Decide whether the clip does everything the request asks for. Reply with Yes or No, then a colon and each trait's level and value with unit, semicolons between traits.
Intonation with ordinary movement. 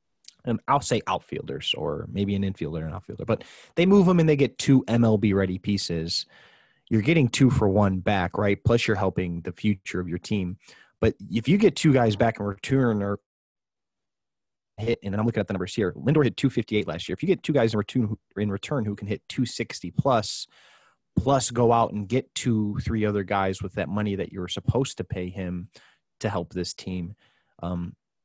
Yes: average, 3.4 semitones